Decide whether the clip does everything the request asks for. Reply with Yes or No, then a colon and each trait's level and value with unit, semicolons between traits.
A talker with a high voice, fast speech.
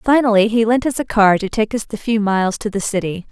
Yes: high, 215 Hz; fast, 270 wpm